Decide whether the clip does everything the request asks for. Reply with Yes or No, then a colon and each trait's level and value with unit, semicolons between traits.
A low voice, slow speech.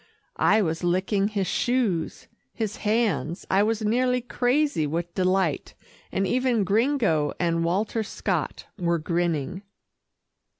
No: high, 195 Hz; slow, 120 wpm